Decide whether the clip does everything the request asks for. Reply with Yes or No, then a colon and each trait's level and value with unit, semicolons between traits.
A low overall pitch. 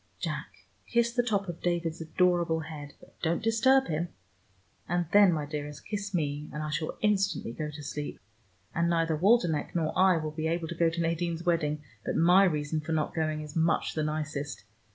No: medium, 165 Hz